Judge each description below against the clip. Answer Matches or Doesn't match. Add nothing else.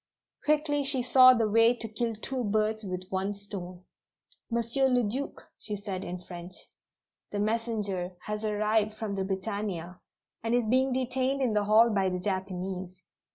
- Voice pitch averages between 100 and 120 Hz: Doesn't match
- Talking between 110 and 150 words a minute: Doesn't match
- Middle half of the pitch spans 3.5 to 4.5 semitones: Matches